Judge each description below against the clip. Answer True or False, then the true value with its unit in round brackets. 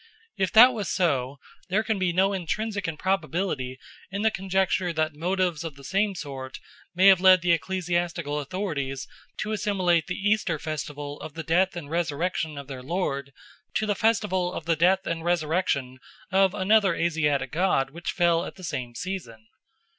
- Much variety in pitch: False (4.2 semitones)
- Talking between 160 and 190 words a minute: True (170 wpm)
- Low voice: False (175 Hz)